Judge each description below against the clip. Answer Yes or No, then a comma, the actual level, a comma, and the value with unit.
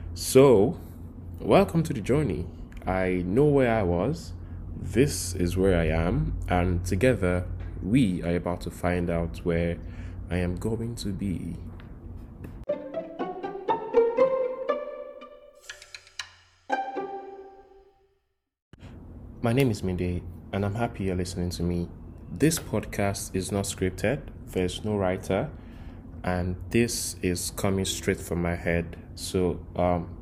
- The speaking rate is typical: No, slow, 115 wpm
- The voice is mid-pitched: No, very low, 90 Hz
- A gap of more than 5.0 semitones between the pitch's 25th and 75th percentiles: Yes, wide, 5.4 semitones